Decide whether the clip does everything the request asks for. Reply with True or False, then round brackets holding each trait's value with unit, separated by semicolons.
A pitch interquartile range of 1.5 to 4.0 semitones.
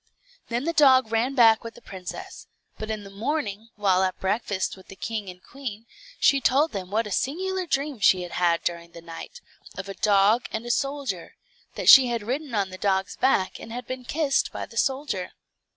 False (5.6 semitones)